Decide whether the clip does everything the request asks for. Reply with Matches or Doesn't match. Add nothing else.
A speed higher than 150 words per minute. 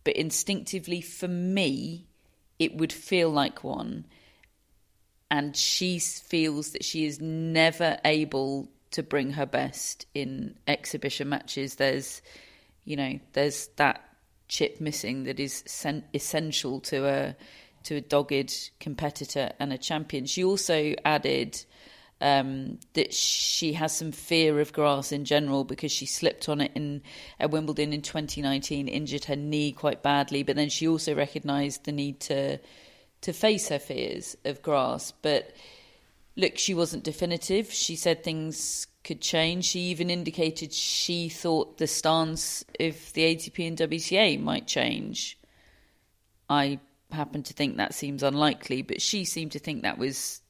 Doesn't match